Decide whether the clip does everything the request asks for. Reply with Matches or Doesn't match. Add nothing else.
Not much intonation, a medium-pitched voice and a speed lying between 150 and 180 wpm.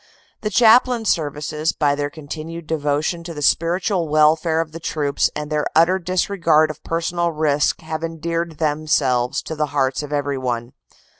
Matches